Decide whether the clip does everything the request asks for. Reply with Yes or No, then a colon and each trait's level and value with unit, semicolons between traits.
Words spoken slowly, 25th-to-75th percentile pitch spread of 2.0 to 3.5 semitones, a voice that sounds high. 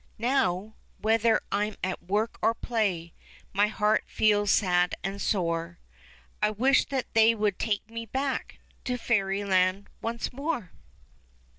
Yes: slow, 130 wpm; average, 3.0 semitones; high, 210 Hz